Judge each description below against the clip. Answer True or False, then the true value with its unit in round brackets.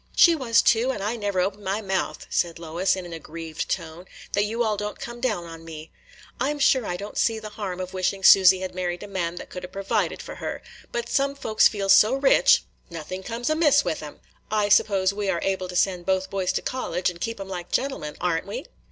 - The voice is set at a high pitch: True (195 Hz)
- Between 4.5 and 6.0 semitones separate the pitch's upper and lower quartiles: False (3.8 semitones)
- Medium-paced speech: False (235 wpm)